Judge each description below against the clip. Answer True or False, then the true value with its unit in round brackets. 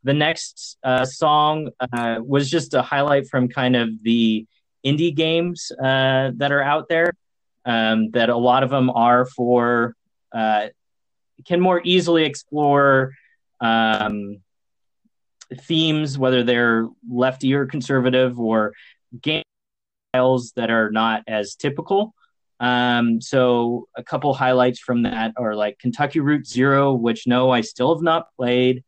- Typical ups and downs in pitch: True (3.5 semitones)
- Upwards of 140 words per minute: False (135 wpm)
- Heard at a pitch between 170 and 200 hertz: False (125 Hz)